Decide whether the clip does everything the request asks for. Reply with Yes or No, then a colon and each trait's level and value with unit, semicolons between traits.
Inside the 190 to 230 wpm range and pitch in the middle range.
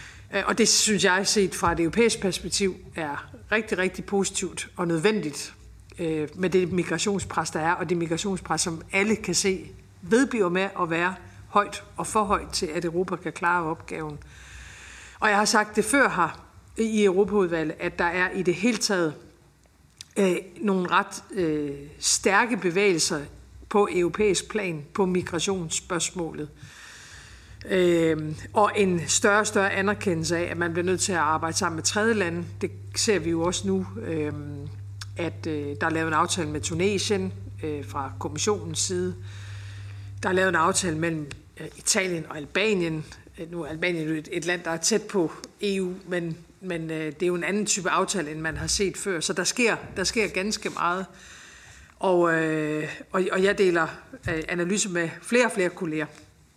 No: average, 175 wpm; medium, 175 Hz